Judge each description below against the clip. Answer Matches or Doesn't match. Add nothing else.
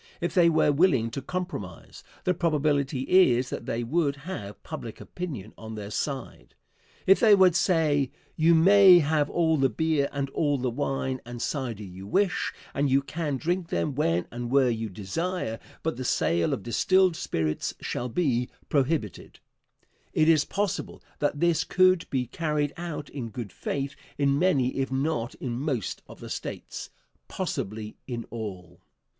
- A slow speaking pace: Doesn't match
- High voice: Doesn't match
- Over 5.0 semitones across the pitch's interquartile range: Matches